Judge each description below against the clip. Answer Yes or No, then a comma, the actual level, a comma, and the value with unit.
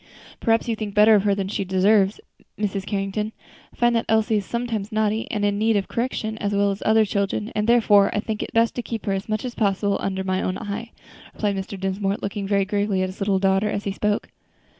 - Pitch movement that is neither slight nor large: No, narrow, 1.9 semitones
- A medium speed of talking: No, fast, 235 wpm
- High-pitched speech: Yes, high, 205 Hz